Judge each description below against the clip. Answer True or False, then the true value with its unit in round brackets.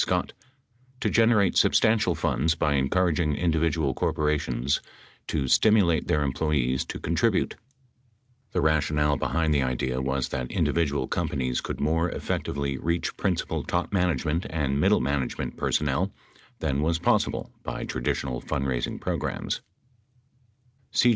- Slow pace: True (120 wpm)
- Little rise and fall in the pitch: False (3.5 semitones)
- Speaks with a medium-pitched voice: False (75 Hz)